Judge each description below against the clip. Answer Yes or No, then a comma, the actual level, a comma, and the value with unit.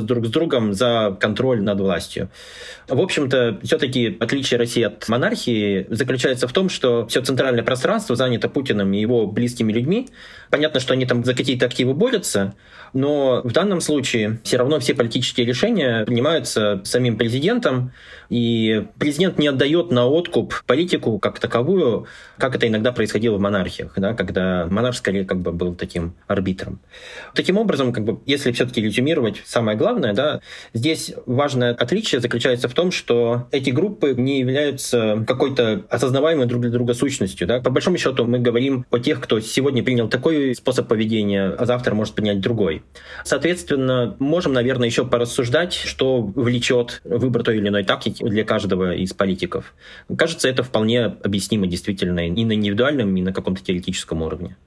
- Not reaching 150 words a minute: No, fast, 160 wpm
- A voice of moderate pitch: No, low, 120 Hz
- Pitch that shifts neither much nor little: Yes, average, 3.9 semitones